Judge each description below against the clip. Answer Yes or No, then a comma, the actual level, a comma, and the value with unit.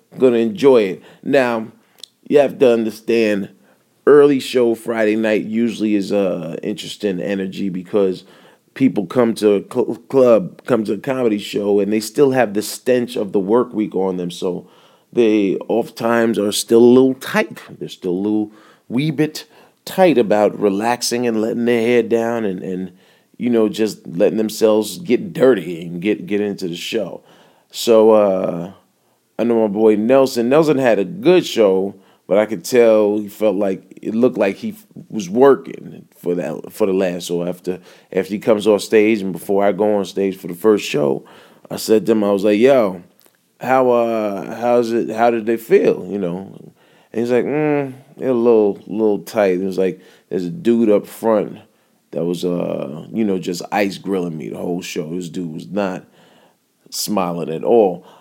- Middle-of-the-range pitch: No, low, 110 Hz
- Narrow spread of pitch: No, average, 3.2 semitones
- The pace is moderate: Yes, average, 190 wpm